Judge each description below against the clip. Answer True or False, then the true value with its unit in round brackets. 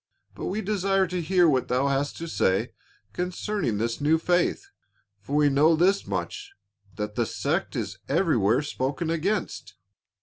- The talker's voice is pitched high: False (165 Hz)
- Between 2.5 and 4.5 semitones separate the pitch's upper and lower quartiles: False (5.3 semitones)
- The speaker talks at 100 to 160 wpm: True (155 wpm)